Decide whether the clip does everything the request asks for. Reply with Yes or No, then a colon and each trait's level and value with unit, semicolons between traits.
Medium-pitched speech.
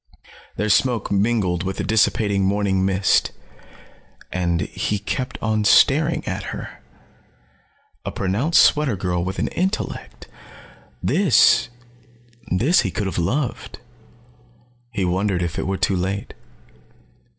No: low, 100 Hz